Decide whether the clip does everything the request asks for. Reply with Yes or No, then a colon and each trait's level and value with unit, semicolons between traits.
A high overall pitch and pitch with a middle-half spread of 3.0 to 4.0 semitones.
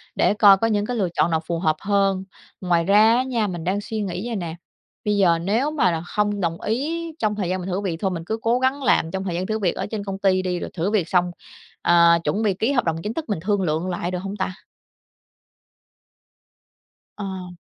Yes: high, 195 Hz; average, 3.4 semitones